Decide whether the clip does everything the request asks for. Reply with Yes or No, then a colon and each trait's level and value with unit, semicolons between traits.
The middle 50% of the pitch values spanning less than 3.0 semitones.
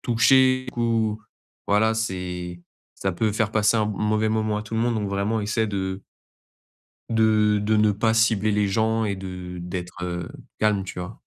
Yes: narrow, 2.5 semitones